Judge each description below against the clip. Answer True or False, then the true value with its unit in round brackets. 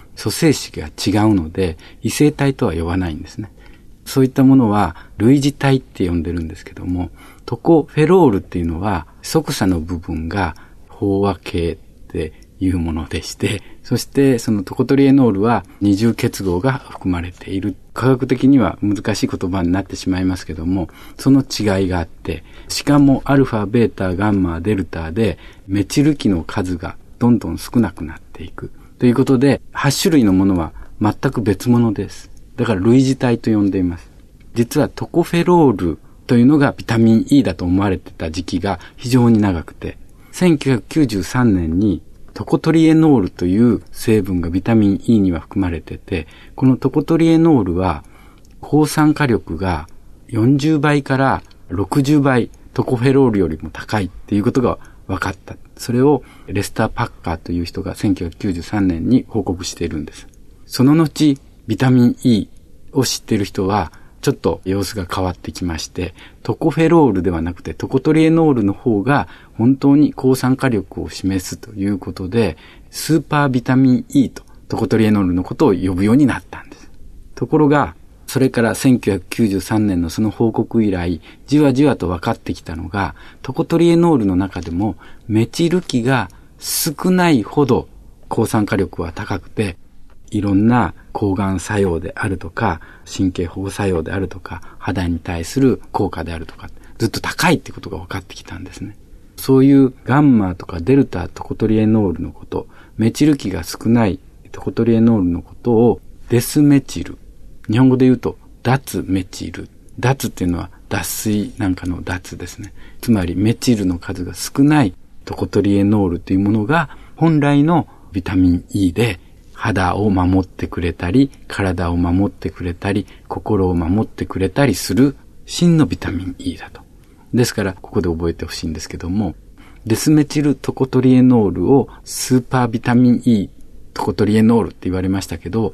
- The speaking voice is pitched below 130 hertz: True (100 Hz)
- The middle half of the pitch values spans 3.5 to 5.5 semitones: False (6.0 semitones)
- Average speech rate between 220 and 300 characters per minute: False (335 characters per minute)